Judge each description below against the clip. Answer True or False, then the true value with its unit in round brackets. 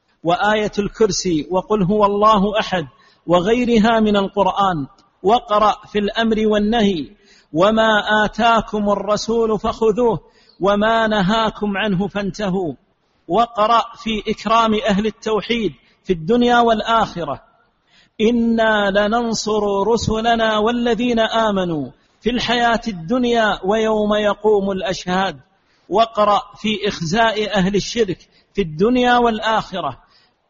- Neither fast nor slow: True (95 wpm)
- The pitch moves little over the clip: True (2.2 semitones)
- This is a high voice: True (215 Hz)